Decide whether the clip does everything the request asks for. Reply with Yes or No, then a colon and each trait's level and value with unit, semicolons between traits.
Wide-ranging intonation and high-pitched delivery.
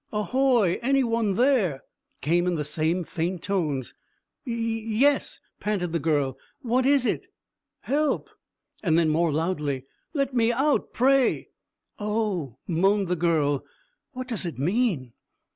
Yes: wide, 6.9 semitones; high, 195 Hz